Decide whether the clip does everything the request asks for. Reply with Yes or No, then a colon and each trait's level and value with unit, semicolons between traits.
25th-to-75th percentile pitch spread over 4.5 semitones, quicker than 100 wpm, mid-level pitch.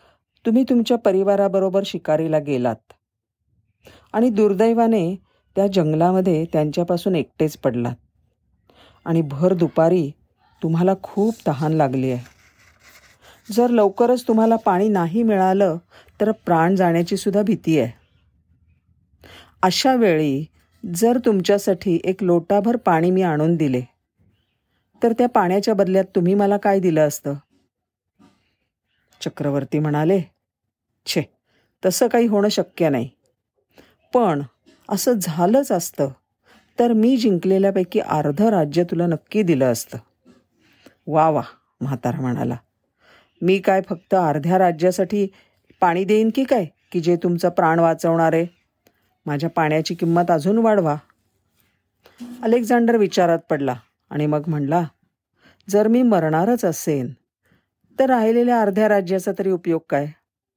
Yes: average, 5.3 semitones; average, 110 wpm; medium, 175 Hz